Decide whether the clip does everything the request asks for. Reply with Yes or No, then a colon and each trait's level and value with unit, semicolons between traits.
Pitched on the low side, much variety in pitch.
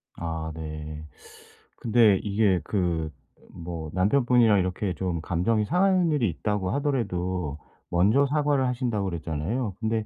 Yes: low, 100 Hz; wide, 6.0 semitones